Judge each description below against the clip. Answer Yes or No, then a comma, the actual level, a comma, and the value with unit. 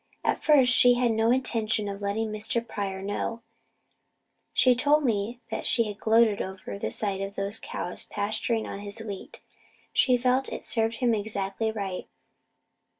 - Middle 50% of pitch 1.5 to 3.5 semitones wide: Yes, average, 2.9 semitones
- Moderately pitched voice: No, high, 220 Hz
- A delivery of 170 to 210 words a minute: No, average, 160 wpm